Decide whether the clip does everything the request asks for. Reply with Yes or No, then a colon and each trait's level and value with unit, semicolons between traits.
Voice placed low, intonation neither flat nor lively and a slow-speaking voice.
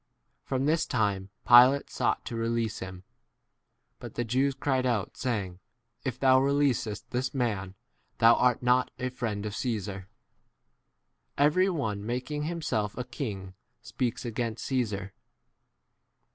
Yes: low, 120 Hz; average, 3.9 semitones; slow, 130 wpm